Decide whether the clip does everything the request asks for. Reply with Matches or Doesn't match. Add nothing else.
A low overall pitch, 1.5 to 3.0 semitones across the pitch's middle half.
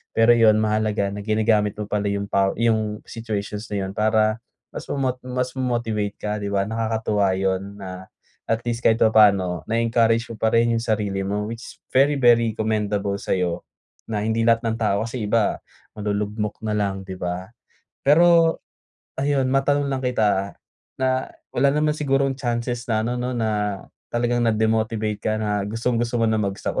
Matches